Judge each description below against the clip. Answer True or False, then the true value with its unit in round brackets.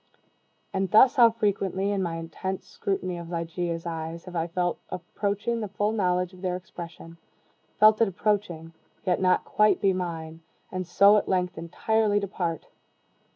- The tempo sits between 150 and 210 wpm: True (155 wpm)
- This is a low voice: False (185 Hz)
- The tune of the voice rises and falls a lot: False (3.1 semitones)